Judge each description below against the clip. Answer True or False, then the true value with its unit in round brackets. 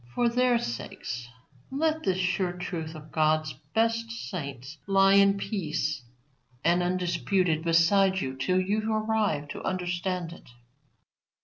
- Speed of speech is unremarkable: False (125 wpm)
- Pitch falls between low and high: True (180 Hz)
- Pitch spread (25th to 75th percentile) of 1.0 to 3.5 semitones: False (4.4 semitones)